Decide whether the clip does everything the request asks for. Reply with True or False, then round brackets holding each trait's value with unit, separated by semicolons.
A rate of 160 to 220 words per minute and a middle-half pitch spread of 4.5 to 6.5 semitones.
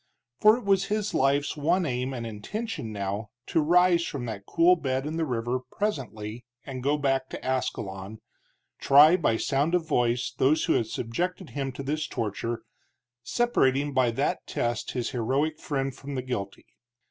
True (170 wpm; 5.0 semitones)